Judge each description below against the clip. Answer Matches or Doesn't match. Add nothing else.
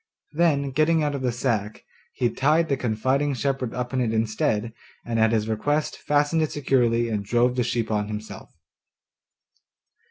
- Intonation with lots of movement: Doesn't match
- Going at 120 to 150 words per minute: Doesn't match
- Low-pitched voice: Matches